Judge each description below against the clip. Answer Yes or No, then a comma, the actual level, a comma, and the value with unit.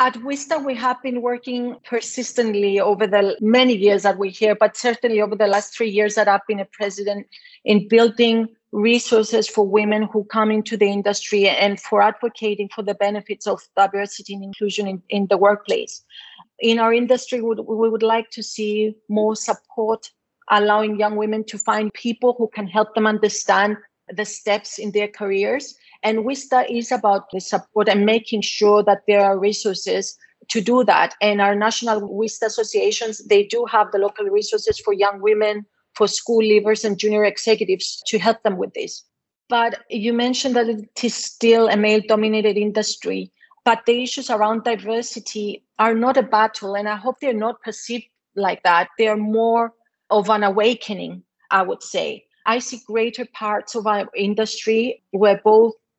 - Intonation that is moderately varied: No, narrow, 2.0 semitones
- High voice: Yes, high, 215 Hz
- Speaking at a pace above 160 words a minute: Yes, average, 175 wpm